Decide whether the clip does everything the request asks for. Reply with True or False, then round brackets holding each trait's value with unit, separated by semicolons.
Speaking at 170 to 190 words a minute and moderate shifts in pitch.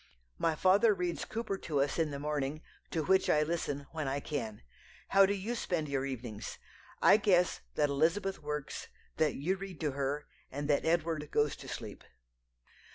True (175 wpm; 4.5 semitones)